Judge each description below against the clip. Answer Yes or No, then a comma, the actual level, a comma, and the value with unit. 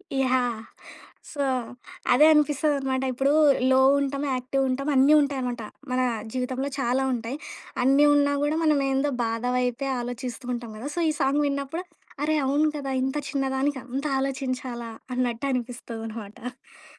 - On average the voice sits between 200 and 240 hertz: No, very high, 265 Hz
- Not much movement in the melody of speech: Yes, narrow, 2.2 semitones